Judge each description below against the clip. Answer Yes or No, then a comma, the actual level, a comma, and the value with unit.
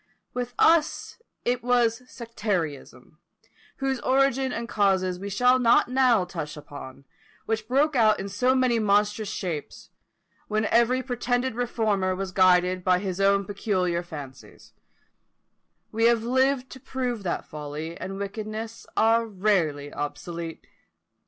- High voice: Yes, high, 215 Hz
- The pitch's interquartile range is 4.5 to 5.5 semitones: Yes, average, 5.2 semitones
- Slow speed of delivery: Yes, slow, 130 wpm